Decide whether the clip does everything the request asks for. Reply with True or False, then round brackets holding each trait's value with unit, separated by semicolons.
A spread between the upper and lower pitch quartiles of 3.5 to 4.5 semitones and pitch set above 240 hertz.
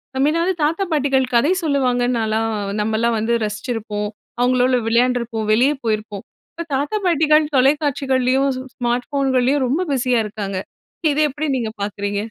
True (4.0 semitones; 250 Hz)